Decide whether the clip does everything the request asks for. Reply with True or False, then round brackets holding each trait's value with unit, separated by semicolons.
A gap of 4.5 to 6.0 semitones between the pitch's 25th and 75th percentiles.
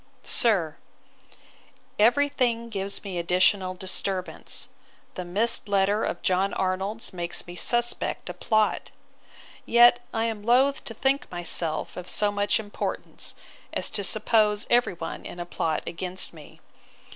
False (4.0 semitones)